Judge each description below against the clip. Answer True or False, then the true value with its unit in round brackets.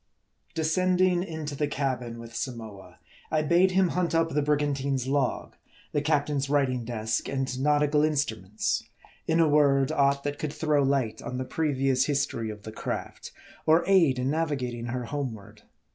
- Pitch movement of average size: True (3.4 semitones)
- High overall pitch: False (140 Hz)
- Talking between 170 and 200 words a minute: False (160 wpm)